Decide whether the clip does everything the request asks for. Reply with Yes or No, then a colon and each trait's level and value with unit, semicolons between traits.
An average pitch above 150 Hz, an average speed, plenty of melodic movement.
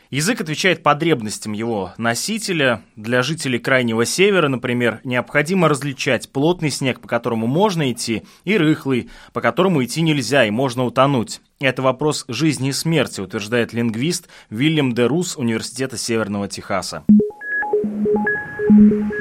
No: low, 135 Hz; average, 120 wpm; wide, 6.1 semitones